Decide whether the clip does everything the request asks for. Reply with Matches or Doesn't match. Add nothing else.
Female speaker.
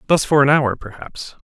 Doesn't match